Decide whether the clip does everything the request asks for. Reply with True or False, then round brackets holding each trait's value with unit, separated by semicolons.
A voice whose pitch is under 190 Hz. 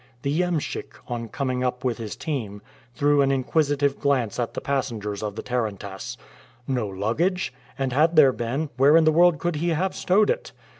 True (135 Hz)